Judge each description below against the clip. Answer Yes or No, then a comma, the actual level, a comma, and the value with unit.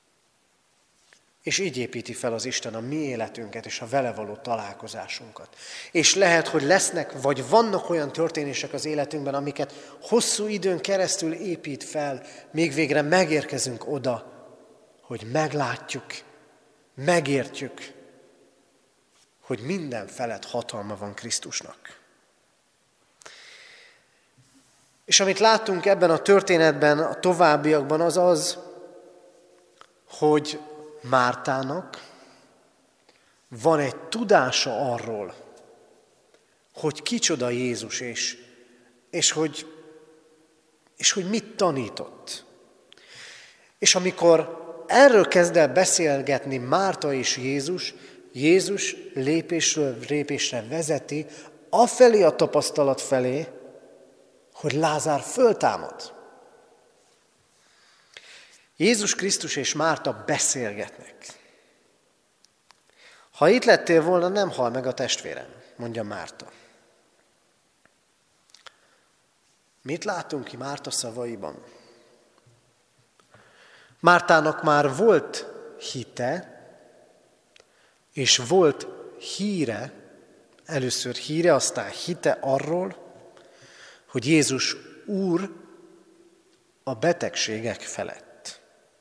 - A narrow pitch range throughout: No, wide, 5.6 semitones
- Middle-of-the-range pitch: Yes, medium, 155 Hz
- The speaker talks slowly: Yes, slow, 85 wpm